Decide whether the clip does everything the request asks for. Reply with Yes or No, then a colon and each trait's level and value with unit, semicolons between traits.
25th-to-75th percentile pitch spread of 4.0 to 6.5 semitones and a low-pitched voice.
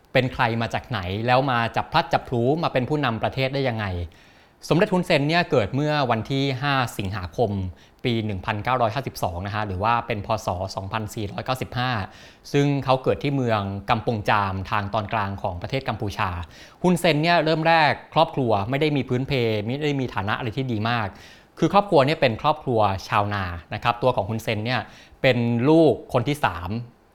Yes: average, 4.4 semitones; low, 120 Hz